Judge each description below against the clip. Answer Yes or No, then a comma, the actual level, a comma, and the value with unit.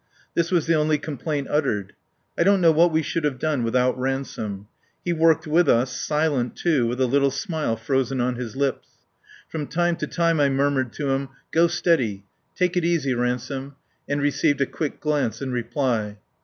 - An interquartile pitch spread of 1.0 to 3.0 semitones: No, average, 4.1 semitones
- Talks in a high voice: No, medium, 140 Hz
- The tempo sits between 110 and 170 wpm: No, average, 185 wpm